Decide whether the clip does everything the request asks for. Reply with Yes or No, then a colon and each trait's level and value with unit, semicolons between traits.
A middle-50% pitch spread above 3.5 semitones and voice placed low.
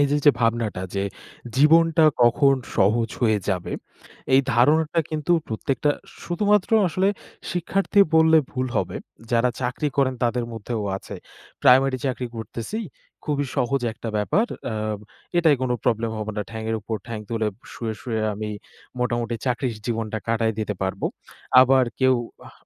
Yes: average, 4.6 semitones; low, 125 Hz